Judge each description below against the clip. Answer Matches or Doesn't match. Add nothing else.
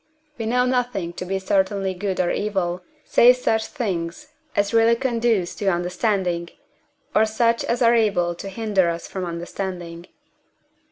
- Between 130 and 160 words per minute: Matches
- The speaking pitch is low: Doesn't match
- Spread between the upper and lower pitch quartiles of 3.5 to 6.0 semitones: Matches